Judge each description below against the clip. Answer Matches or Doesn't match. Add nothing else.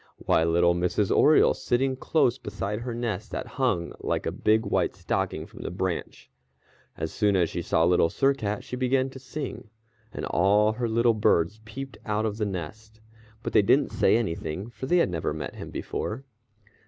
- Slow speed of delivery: Doesn't match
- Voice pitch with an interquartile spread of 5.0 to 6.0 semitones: Matches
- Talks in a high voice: Doesn't match